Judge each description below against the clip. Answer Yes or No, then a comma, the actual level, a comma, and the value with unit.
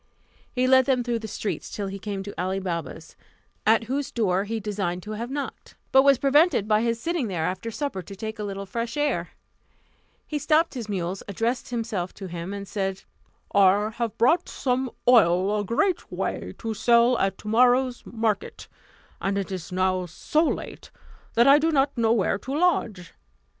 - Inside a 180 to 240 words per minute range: Yes, average, 185 wpm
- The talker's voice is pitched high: Yes, high, 220 Hz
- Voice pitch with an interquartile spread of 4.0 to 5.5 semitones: Yes, average, 4.6 semitones